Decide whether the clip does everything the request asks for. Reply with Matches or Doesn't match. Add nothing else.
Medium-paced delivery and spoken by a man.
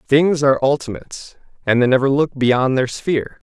Matches